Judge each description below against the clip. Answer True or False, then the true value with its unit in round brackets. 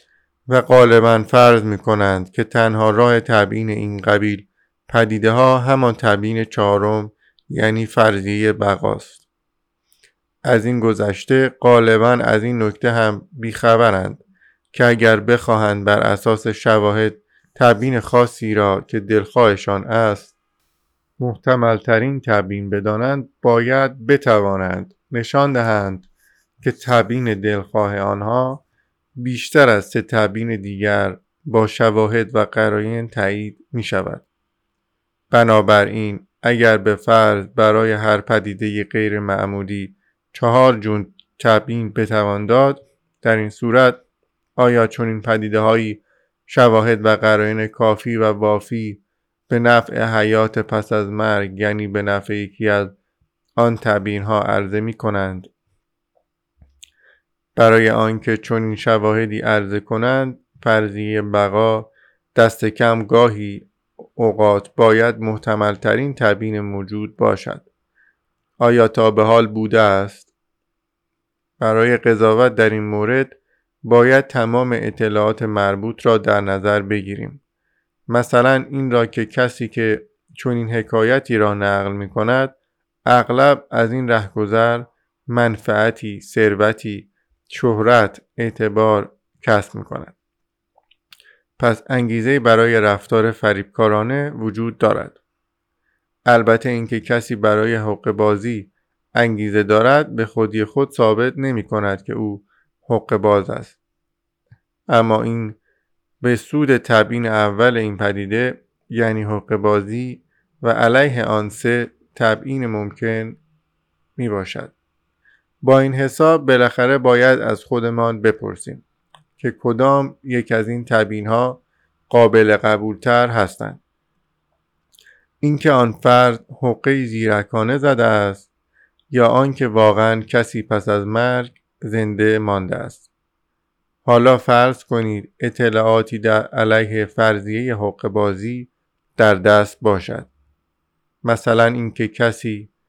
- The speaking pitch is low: True (110 Hz)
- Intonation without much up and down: True (2.2 semitones)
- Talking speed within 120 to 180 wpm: False (110 wpm)